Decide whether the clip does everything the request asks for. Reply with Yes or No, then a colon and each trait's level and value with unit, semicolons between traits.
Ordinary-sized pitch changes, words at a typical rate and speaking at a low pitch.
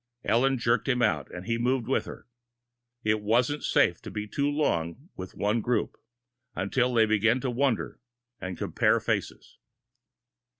Yes: average, 3.8 semitones; average, 155 wpm; low, 115 Hz